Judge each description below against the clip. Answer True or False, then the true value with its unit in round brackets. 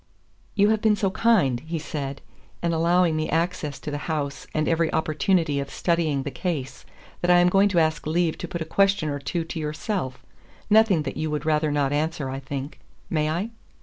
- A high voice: False (160 Hz)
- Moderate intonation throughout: True (3.3 semitones)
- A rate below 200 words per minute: False (205 wpm)